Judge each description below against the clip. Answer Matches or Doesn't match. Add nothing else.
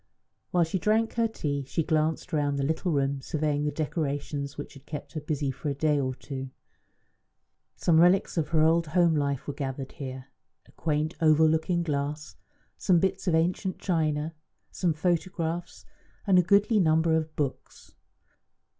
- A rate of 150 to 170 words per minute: Matches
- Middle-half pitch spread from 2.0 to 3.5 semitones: Matches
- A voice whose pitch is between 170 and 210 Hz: Doesn't match